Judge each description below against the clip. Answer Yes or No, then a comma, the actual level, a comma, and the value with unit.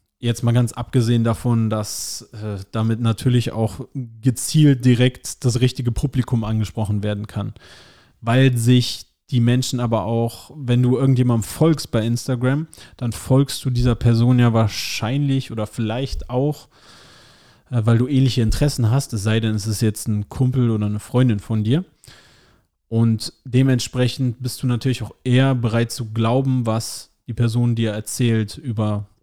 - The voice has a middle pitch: No, low, 120 Hz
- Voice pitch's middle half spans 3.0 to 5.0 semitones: No, narrow, 2.4 semitones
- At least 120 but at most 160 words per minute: Yes, average, 155 wpm